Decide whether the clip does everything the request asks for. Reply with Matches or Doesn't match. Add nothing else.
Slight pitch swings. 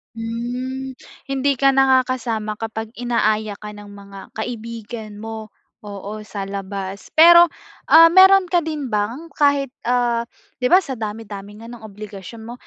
Doesn't match